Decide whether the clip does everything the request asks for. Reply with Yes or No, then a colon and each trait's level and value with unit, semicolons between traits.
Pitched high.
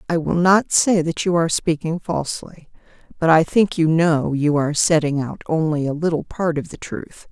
No: medium, 160 Hz